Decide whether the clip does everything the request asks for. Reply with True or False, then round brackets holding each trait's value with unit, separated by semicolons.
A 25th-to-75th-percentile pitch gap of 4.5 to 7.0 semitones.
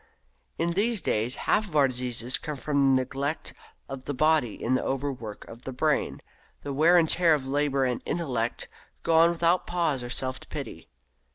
False (4.0 semitones)